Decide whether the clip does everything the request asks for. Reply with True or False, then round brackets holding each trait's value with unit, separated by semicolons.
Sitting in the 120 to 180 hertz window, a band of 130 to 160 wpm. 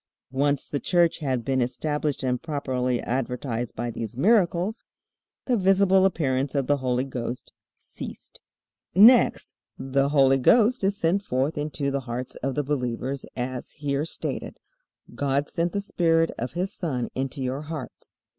True (140 Hz; 150 wpm)